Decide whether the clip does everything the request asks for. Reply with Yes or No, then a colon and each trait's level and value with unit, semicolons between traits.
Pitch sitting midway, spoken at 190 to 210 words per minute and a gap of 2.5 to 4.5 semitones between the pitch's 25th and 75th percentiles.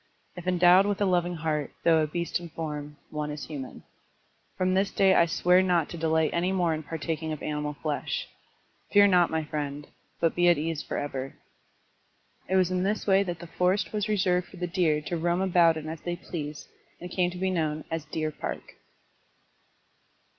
Yes: medium, 170 Hz; average, 195 wpm; average, 2.8 semitones